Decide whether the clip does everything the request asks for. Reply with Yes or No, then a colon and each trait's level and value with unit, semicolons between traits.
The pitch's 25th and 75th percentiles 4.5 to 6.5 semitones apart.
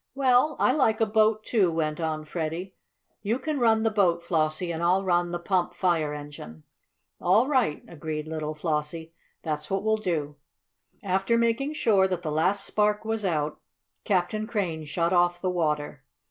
Yes: wide, 5.5 semitones